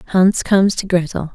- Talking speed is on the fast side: No, average, 180 wpm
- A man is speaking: No, female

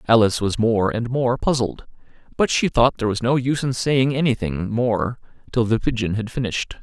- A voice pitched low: Yes, low, 120 Hz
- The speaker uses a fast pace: No, average, 195 wpm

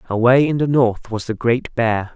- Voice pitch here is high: No, low, 120 Hz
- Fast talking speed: Yes, fast, 220 wpm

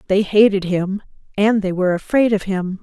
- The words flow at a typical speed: Yes, average, 190 wpm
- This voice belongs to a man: No, female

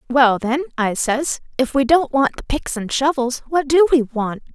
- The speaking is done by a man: No, female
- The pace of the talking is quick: Yes, fast, 210 wpm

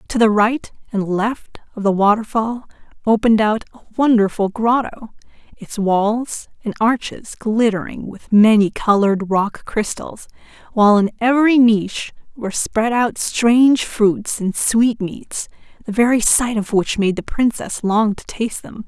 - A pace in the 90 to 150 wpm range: Yes, average, 145 wpm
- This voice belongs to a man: No, female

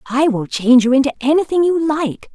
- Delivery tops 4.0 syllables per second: Yes, 5.6 syllables/s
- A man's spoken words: No, female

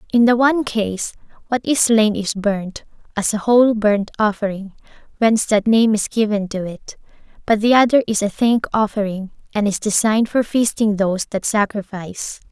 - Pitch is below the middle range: No, high, 215 Hz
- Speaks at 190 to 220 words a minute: No, average, 175 wpm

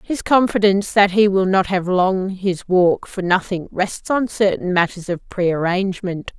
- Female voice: Yes, female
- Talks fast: No, average, 180 wpm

